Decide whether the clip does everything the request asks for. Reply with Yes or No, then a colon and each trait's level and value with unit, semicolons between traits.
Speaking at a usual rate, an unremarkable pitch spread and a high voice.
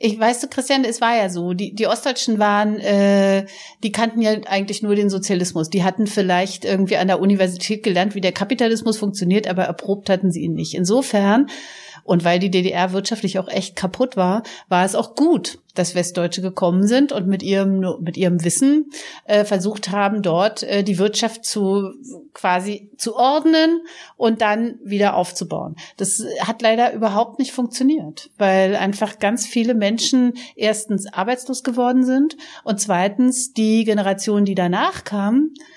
Yes: average, 165 wpm; average, 3.7 semitones; high, 205 Hz